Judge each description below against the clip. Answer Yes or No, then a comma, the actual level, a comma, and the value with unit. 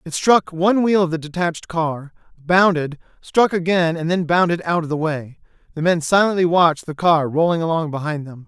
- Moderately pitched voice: Yes, medium, 165 Hz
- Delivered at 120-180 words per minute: No, average, 200 wpm